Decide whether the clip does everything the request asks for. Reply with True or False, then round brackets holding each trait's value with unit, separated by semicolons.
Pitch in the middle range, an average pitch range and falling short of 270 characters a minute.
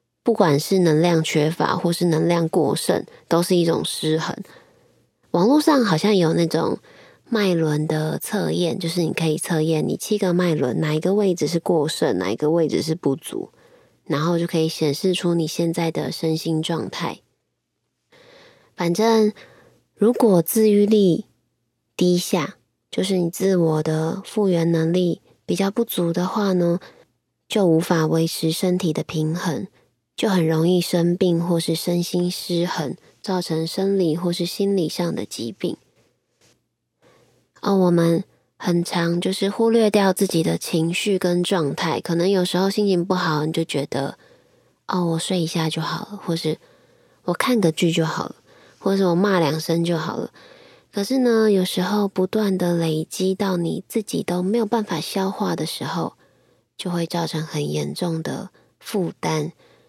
True (175 Hz; 3.2 semitones; 230 characters per minute)